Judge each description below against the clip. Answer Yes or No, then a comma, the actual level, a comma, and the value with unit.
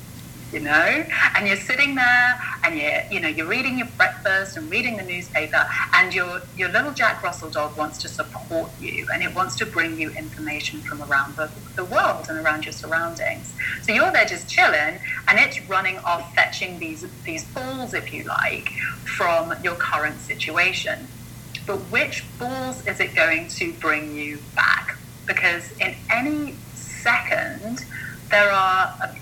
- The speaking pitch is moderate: Yes, medium, 165 Hz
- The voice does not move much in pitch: No, average, 5.3 semitones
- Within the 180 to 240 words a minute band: No, average, 170 wpm